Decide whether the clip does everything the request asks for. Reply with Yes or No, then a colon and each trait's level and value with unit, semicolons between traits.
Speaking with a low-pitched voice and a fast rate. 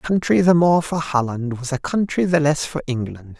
No: medium, 150 Hz; fast, 230 wpm